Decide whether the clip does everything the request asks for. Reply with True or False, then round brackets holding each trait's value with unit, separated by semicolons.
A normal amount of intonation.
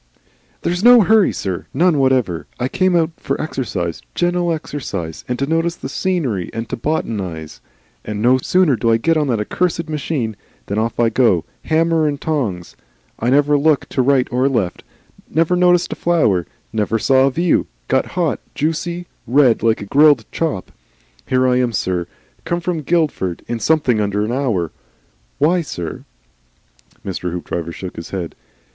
False (7.4 semitones)